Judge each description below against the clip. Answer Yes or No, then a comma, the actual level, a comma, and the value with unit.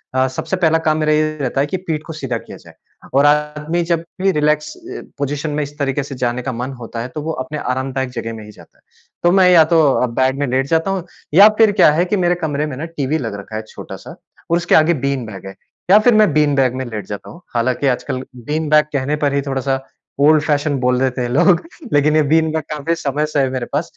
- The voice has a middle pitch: Yes, medium, 145 Hz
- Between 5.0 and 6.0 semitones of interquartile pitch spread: No, average, 3.4 semitones